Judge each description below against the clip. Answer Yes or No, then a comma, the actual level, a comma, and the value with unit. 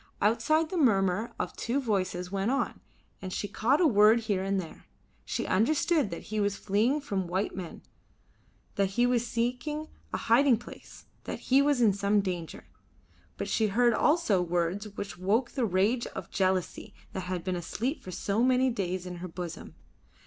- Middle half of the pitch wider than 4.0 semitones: Yes, average, 4.7 semitones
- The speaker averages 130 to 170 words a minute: No, average, 180 wpm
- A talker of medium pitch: No, high, 210 Hz